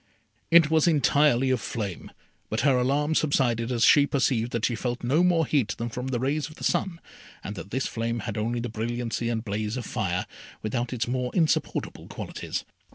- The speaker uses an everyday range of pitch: Yes, average, 3.6 semitones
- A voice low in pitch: Yes, low, 120 Hz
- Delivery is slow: No, average, 195 wpm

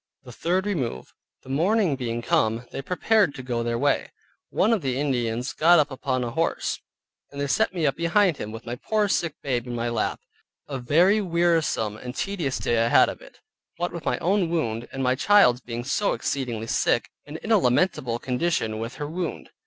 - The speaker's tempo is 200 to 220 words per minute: Yes, fast, 205 wpm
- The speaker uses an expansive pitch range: Yes, wide, 6.3 semitones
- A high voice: No, medium, 140 Hz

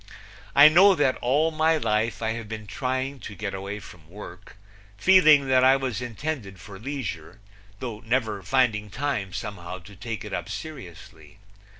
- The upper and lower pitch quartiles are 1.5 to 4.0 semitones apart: No, average, 5.2 semitones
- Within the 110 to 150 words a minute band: No, average, 165 wpm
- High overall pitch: No, low, 115 Hz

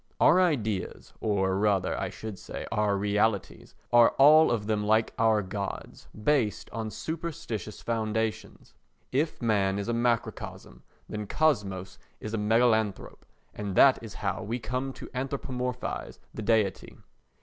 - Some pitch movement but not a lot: Yes, average, 3.2 semitones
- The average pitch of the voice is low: Yes, low, 110 Hz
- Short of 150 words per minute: Yes, average, 140 wpm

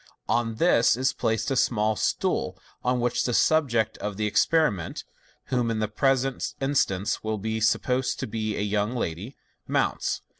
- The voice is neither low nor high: No, low, 115 Hz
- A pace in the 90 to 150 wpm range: No, average, 165 wpm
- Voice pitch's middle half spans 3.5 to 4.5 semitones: No, average, 3.1 semitones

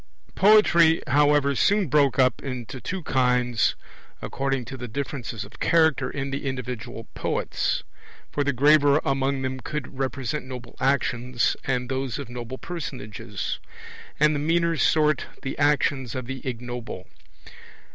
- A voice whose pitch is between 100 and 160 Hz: Yes, low, 135 Hz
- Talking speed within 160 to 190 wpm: No, slow, 135 wpm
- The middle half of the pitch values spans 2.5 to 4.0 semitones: Yes, average, 2.9 semitones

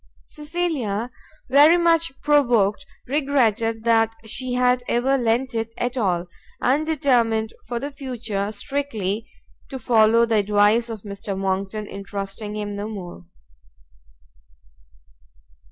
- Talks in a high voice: Yes, high, 230 Hz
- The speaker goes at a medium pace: No, slow, 120 wpm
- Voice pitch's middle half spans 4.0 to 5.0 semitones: Yes, average, 4.3 semitones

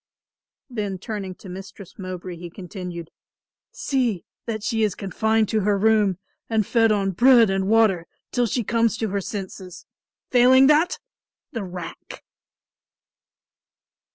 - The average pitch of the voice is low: No, high, 205 Hz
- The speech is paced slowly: Yes, slow, 130 wpm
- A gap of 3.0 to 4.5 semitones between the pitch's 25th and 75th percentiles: Yes, average, 3.3 semitones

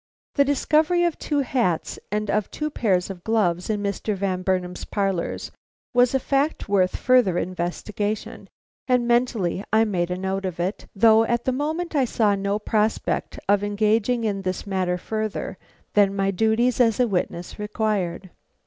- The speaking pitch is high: Yes, high, 210 Hz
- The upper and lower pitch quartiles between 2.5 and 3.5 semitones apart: No, average, 4.0 semitones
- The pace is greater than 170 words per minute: No, average, 165 wpm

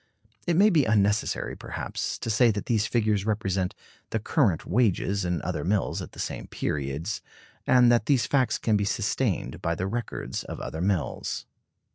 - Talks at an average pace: Yes, average, 170 wpm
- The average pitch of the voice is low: Yes, low, 105 Hz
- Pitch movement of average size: Yes, average, 4.1 semitones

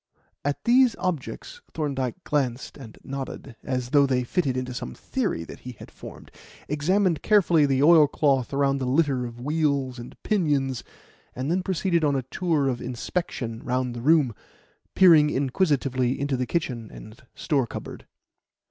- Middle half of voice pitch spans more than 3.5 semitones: Yes, average, 4.2 semitones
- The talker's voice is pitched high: No, medium, 140 Hz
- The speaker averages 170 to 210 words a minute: No, average, 155 wpm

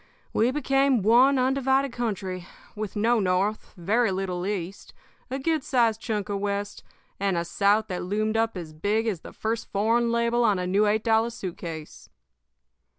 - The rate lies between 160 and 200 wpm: Yes, average, 170 wpm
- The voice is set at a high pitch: Yes, high, 215 Hz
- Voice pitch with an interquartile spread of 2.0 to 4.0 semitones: Yes, average, 3.5 semitones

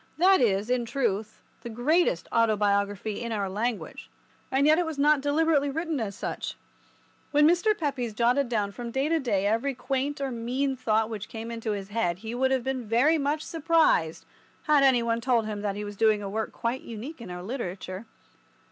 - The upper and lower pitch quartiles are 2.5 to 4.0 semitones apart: No, average, 4.8 semitones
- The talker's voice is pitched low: No, high, 235 Hz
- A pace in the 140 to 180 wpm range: No, average, 195 wpm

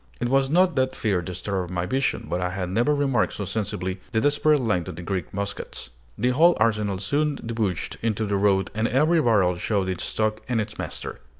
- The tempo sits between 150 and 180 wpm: No, fast, 205 wpm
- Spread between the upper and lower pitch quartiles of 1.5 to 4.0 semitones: No, wide, 5.6 semitones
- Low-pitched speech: Yes, low, 110 Hz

